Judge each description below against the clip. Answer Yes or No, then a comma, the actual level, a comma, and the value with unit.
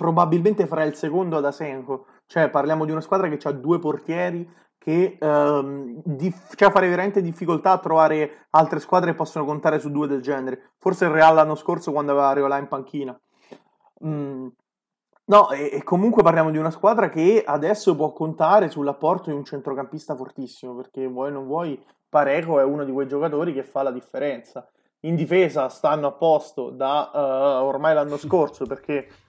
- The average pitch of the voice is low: No, medium, 155 Hz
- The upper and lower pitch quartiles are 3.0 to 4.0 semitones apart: Yes, average, 3.5 semitones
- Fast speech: Yes, fast, 180 wpm